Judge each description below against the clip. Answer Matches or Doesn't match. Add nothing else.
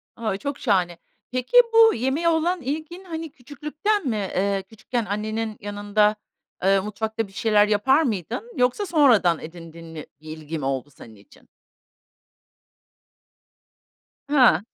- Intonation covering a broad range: Matches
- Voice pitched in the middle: Doesn't match